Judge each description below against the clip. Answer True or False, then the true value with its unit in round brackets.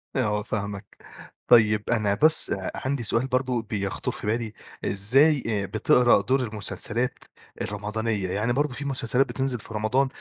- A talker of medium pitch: False (115 Hz)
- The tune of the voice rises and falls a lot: False (3.5 semitones)